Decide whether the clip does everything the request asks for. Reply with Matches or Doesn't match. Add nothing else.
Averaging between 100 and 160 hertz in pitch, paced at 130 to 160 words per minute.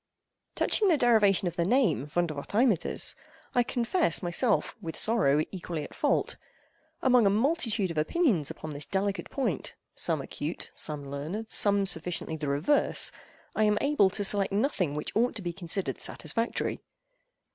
Doesn't match